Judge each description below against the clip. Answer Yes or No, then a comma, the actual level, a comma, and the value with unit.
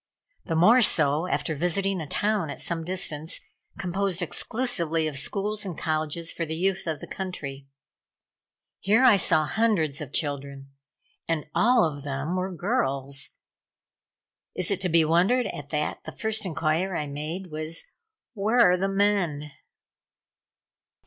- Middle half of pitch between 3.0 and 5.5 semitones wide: Yes, average, 4.4 semitones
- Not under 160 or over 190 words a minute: No, average, 145 wpm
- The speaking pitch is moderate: Yes, medium, 170 Hz